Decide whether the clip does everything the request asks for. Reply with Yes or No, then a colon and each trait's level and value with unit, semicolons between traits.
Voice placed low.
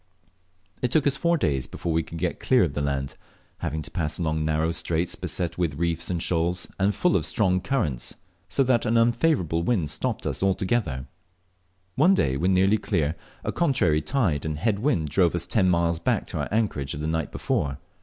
Yes: very low, 85 Hz